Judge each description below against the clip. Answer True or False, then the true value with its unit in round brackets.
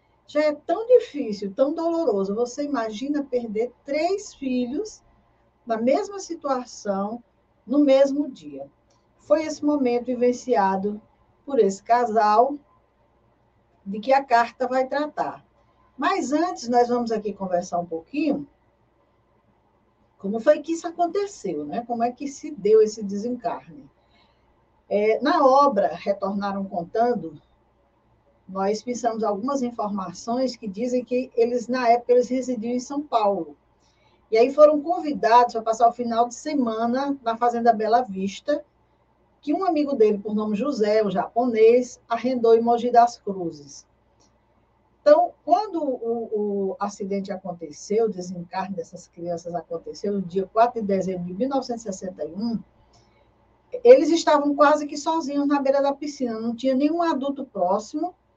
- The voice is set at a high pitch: True (235 Hz)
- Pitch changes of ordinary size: False (6.1 semitones)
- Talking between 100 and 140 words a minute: True (135 wpm)